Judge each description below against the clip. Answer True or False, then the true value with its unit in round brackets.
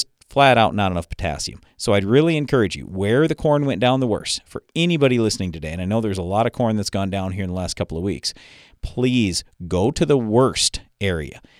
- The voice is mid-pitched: False (100 Hz)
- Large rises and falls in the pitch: True (5.7 semitones)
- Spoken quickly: True (235 wpm)